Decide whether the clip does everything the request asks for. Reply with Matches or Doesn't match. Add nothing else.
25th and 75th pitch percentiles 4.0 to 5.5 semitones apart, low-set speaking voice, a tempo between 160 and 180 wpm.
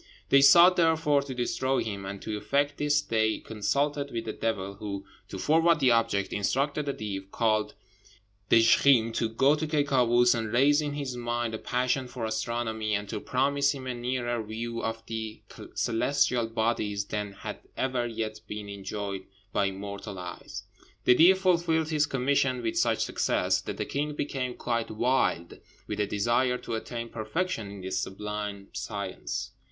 Matches